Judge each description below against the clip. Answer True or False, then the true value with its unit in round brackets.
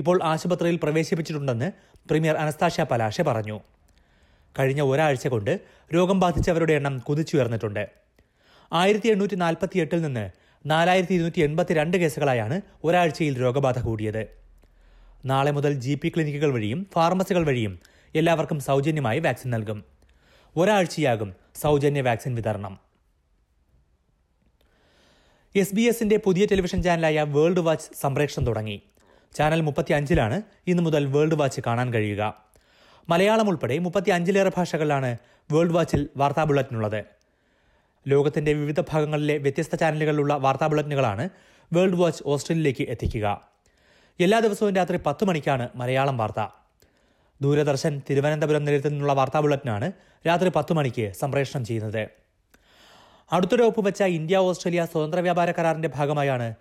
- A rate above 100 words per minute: True (110 wpm)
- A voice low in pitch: False (150 Hz)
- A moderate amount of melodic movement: False (5.7 semitones)